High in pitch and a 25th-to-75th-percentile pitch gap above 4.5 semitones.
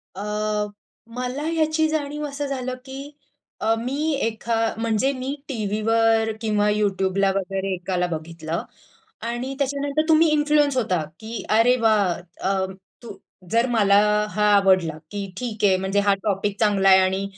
Yes: high, 220 Hz; average, 5.2 semitones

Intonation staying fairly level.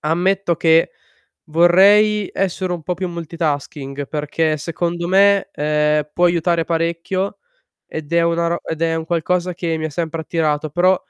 Yes: narrow, 2.1 semitones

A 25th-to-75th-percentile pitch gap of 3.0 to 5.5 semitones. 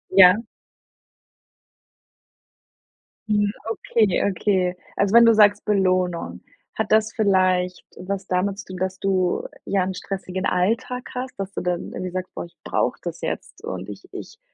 No: narrow, 2.4 semitones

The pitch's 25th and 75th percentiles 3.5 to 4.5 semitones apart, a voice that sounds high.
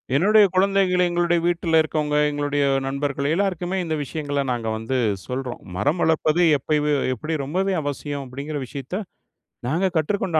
No: average, 3.8 semitones; medium, 155 Hz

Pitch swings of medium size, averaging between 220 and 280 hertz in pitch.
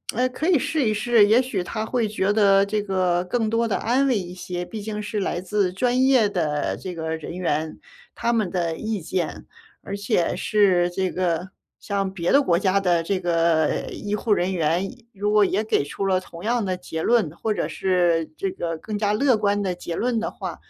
No: average, 3.6 semitones; high, 195 Hz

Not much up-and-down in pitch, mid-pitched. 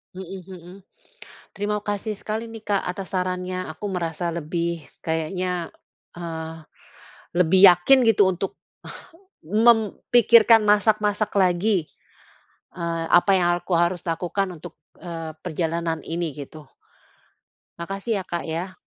No: average, 3.2 semitones; medium, 180 Hz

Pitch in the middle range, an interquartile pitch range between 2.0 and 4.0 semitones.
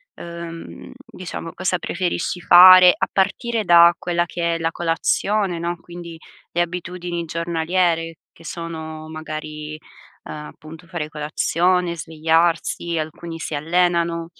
No: medium, 170 Hz; narrow, 1.4 semitones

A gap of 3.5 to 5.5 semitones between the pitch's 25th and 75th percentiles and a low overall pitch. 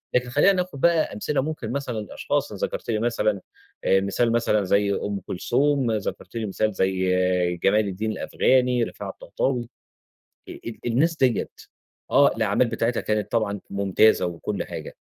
Yes: average, 4.1 semitones; low, 110 Hz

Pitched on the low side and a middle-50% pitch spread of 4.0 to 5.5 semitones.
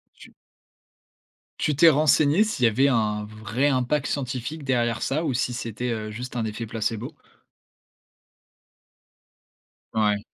Yes: low, 125 Hz; average, 4.3 semitones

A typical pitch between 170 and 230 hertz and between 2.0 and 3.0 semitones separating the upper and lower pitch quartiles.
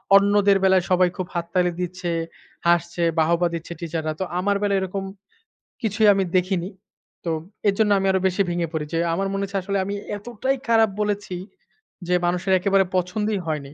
Yes: high, 190 Hz; narrow, 2.5 semitones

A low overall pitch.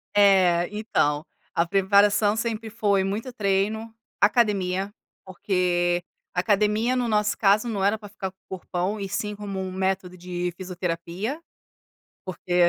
No: high, 195 Hz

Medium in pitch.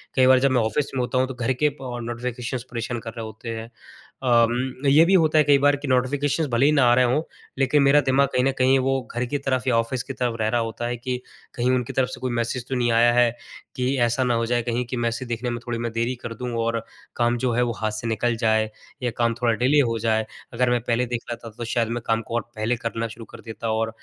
No: low, 120 Hz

